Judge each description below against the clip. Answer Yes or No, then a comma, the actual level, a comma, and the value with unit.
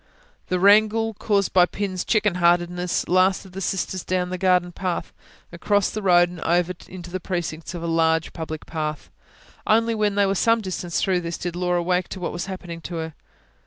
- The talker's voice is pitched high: No, medium, 180 Hz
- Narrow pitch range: Yes, narrow, 2.0 semitones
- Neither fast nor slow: Yes, average, 195 wpm